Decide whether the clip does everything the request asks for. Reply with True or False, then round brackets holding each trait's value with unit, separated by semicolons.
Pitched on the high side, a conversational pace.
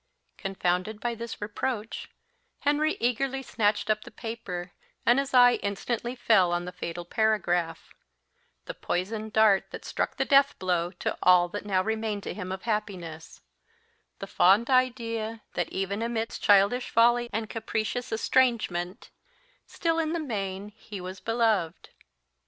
True (215 Hz; 145 wpm)